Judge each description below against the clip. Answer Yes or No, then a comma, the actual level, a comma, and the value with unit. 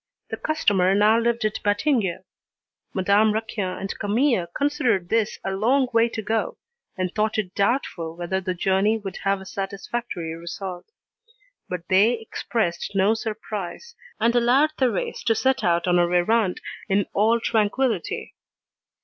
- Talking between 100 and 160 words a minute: Yes, average, 145 wpm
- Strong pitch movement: No, average, 3.7 semitones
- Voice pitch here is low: No, high, 205 Hz